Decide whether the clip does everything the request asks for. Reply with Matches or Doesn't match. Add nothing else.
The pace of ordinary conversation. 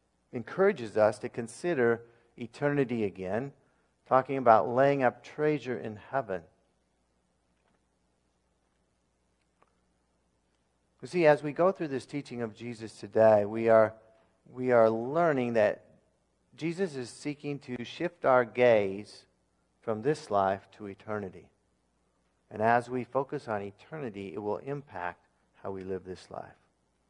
Doesn't match